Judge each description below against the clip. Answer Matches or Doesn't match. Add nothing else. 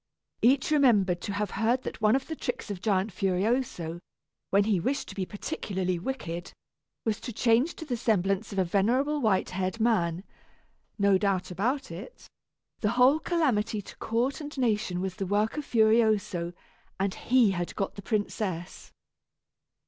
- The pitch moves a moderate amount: Matches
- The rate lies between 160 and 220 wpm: Matches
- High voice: Matches